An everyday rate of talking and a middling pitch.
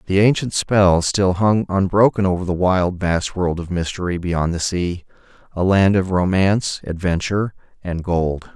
No: average, 155 wpm; very low, 90 Hz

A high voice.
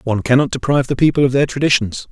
No: low, 130 Hz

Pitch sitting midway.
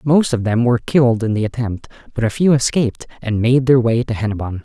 No: low, 120 Hz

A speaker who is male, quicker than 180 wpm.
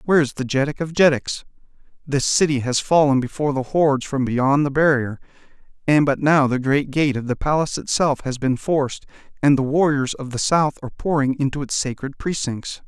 Yes: male; average, 195 wpm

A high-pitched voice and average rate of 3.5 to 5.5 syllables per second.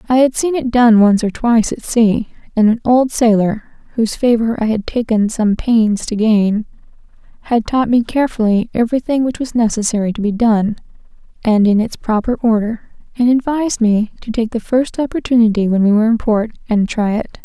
Yes: high, 225 Hz; 5.3 syllables/s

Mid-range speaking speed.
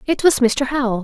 No: fast, 235 wpm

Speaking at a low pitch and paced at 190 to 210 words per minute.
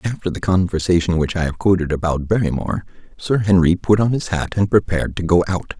Yes: very low, 90 Hz; fast, 205 wpm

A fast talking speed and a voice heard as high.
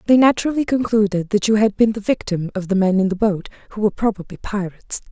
Yes: fast, 225 wpm; high, 205 Hz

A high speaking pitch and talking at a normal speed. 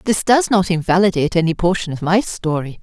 No: medium, 180 Hz; average, 190 wpm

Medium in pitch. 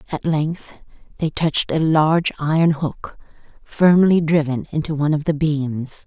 Yes: medium, 155 Hz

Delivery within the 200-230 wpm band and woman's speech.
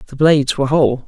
No: fast, 225 wpm; male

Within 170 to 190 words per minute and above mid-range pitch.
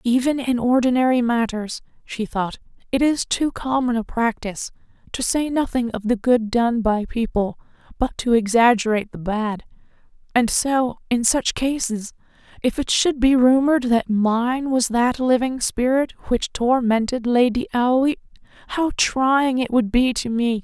No: average, 155 wpm; high, 245 Hz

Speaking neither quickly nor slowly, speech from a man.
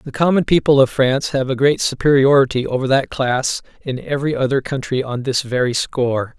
Yes: average, 190 wpm; male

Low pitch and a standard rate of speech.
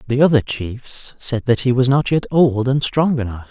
No: low, 125 Hz; fast, 220 wpm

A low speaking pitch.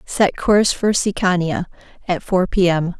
No: medium, 185 Hz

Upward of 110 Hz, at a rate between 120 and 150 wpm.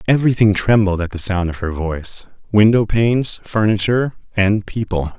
No: low, 105 Hz; average, 140 wpm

